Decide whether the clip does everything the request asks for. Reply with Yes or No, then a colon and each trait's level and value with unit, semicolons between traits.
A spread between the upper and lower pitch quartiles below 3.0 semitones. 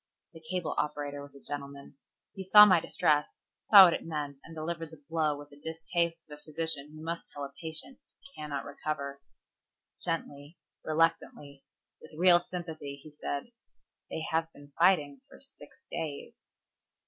Yes: narrow, 2.5 semitones